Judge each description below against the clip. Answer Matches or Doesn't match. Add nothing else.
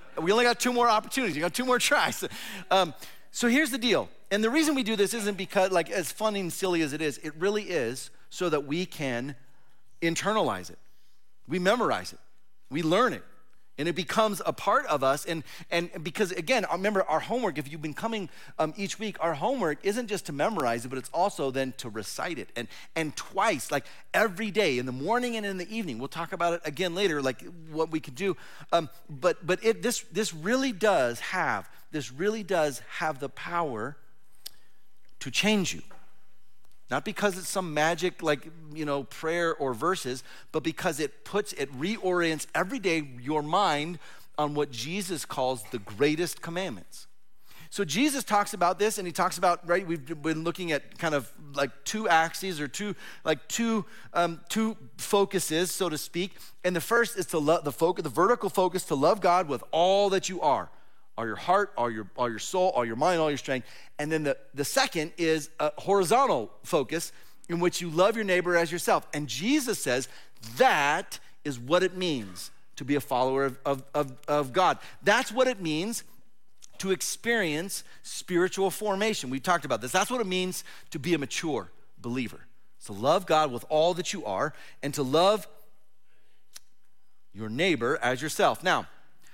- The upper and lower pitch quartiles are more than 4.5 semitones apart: Matches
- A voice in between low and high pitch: Matches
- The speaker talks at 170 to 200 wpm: Matches